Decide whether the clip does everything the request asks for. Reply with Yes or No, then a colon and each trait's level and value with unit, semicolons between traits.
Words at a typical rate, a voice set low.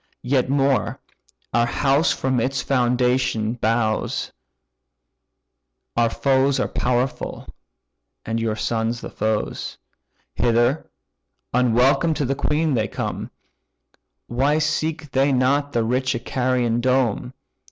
No: slow, 110 wpm; low, 125 Hz